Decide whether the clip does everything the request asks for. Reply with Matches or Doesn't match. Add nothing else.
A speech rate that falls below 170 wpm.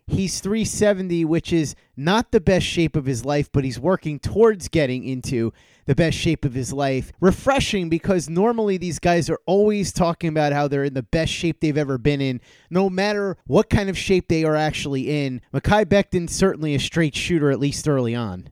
Doesn't match